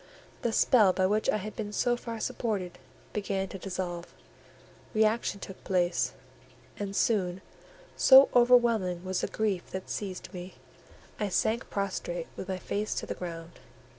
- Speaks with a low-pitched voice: No, high, 195 Hz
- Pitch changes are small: No, average, 3.0 semitones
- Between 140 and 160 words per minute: Yes, average, 150 wpm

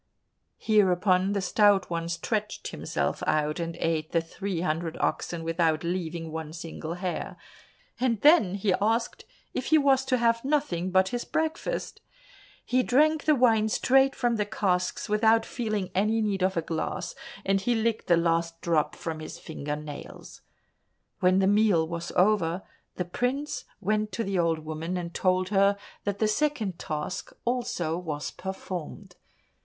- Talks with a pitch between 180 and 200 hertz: Yes, high, 190 Hz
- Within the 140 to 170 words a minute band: Yes, average, 160 wpm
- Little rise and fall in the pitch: No, average, 4.8 semitones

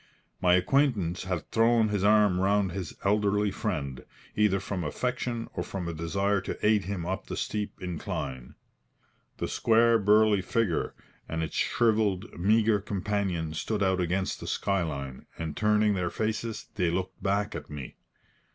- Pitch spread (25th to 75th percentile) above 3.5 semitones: No, average, 3.2 semitones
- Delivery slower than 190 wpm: Yes, average, 155 wpm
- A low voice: Yes, low, 100 Hz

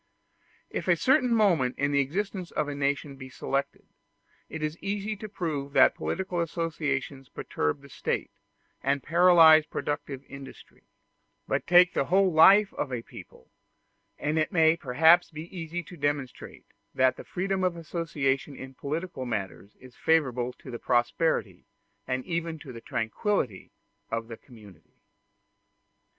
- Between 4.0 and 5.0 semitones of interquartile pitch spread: Yes, average, 4.7 semitones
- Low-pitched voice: No, medium, 150 Hz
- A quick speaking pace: No, average, 145 wpm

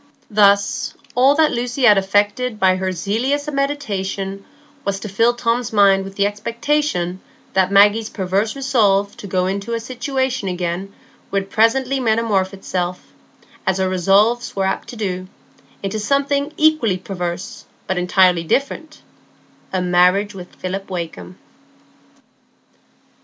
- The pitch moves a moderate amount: Yes, average, 4.2 semitones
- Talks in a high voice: Yes, high, 200 Hz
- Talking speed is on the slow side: Yes, slow, 130 wpm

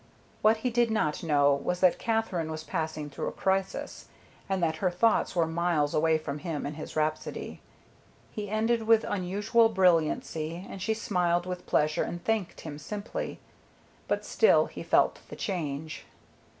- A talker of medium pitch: Yes, medium, 175 Hz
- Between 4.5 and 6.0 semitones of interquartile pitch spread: Yes, average, 5.0 semitones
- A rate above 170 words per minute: No, average, 165 wpm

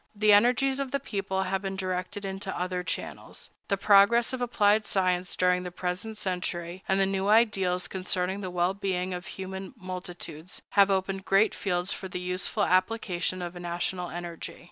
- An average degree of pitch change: No, narrow, 1.9 semitones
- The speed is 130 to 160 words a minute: No, average, 170 wpm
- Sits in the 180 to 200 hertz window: Yes, high, 190 Hz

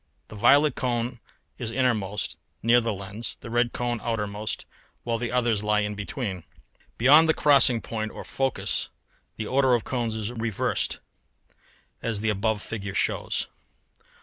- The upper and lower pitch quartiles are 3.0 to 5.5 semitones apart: No, narrow, 2.6 semitones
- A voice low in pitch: Yes, low, 115 Hz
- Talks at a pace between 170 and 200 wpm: No, average, 145 wpm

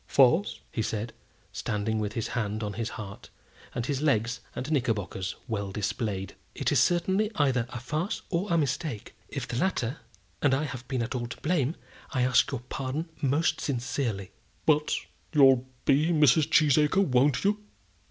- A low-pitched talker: Yes, low, 130 Hz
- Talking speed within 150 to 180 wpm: Yes, average, 165 wpm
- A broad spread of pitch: No, average, 4.9 semitones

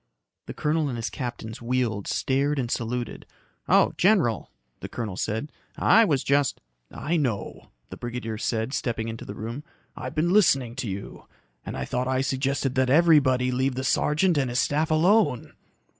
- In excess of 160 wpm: Yes, average, 175 wpm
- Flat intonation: No, average, 4.1 semitones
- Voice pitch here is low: Yes, low, 130 Hz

